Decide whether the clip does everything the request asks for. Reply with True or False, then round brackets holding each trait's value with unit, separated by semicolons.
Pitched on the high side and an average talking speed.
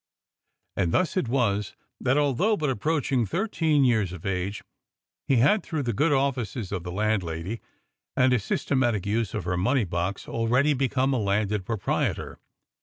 False (115 Hz; 160 wpm)